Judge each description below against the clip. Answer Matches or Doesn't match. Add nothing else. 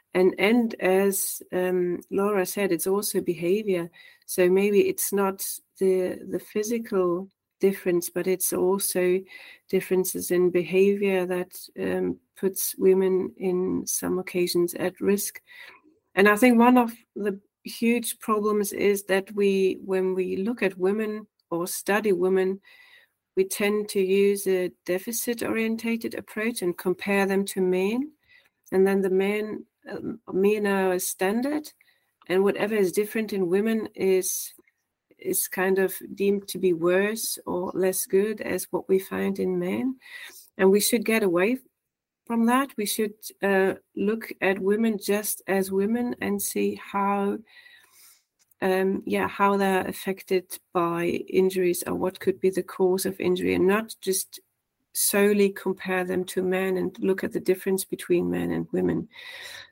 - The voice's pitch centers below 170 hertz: Doesn't match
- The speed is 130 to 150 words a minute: Matches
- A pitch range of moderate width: Doesn't match